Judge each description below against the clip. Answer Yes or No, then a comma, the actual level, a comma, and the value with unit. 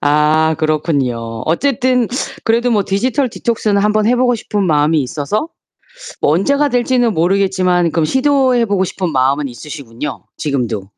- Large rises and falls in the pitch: Yes, wide, 8.0 semitones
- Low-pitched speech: No, medium, 185 Hz